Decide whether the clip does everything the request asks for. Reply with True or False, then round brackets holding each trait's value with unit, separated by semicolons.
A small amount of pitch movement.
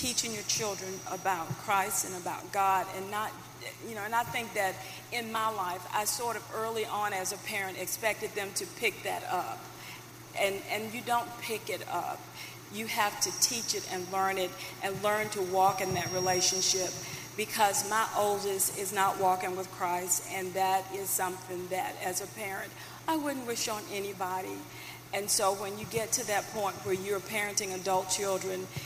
True (2.2 semitones)